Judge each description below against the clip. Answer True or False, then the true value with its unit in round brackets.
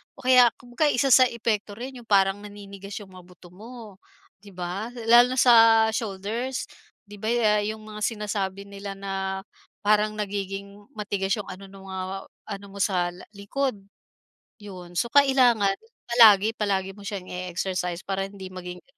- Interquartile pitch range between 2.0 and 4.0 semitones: True (2.8 semitones)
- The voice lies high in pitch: True (205 Hz)